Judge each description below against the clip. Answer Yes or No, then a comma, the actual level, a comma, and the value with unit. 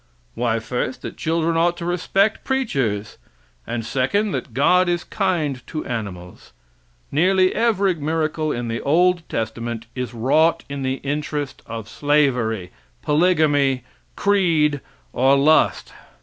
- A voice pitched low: No, medium, 145 Hz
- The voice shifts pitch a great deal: Yes, wide, 5.9 semitones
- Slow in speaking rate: Yes, slow, 125 wpm